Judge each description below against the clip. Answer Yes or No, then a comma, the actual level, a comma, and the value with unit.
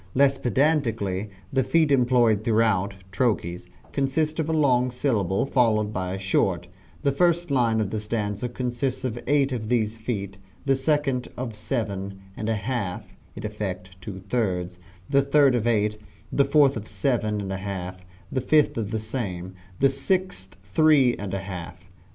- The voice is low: Yes, low, 115 Hz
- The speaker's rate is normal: Yes, average, 165 wpm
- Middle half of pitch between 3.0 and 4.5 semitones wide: No, average, 5.3 semitones